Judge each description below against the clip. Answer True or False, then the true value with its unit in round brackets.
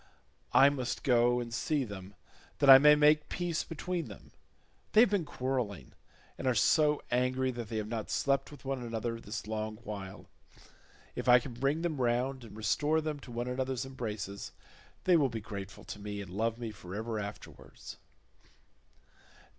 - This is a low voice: True (125 Hz)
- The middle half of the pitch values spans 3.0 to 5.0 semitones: True (4.3 semitones)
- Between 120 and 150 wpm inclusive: False (175 wpm)